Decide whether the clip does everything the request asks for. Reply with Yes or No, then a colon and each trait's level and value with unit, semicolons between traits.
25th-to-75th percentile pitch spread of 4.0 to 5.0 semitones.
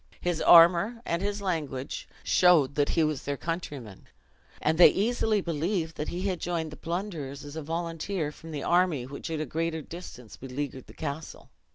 No: average, 3.4 semitones